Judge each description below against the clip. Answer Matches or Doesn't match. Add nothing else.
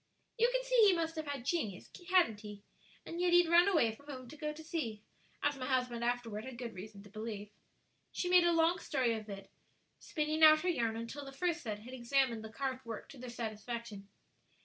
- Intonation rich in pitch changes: Matches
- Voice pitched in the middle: Doesn't match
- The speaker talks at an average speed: Doesn't match